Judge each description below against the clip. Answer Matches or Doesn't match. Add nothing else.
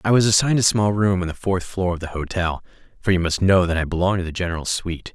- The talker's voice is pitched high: Doesn't match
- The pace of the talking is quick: Matches